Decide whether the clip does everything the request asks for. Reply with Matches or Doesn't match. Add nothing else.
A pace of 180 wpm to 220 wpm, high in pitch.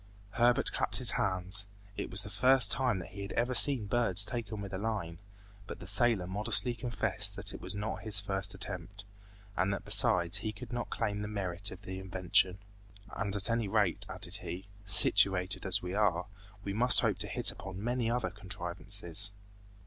Doesn't match